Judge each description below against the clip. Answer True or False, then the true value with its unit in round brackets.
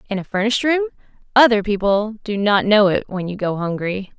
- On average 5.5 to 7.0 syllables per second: True (5.7 syllables/s)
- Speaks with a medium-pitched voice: False (210 Hz)